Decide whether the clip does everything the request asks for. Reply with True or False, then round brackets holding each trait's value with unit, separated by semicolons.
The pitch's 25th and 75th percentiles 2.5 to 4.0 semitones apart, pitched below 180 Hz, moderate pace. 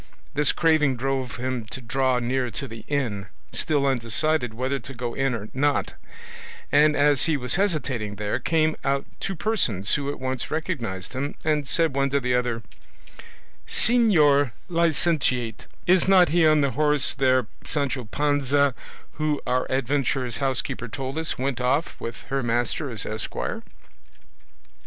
True (3.4 semitones; 135 Hz; 150 wpm)